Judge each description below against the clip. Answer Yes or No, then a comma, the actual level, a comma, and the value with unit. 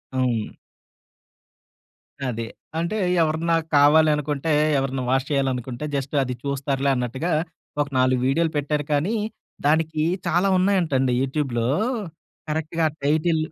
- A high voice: No, medium, 145 Hz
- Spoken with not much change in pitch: No, average, 3.3 semitones